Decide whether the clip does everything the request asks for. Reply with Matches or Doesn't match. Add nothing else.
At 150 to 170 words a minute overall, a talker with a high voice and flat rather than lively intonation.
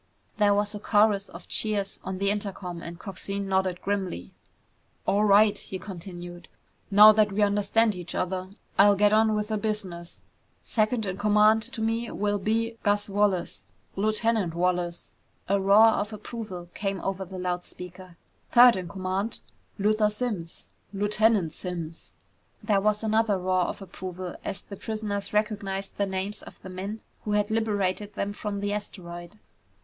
Matches